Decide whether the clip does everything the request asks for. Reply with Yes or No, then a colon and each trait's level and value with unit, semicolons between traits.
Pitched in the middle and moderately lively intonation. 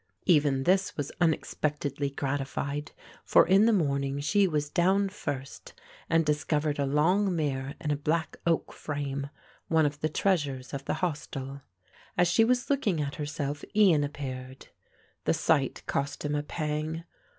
Yes: medium, 150 Hz; average, 3.2 semitones